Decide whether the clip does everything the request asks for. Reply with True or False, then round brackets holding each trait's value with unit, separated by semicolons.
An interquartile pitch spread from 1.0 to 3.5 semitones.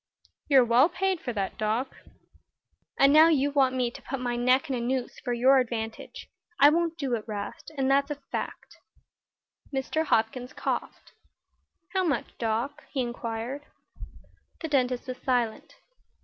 True (3.0 semitones)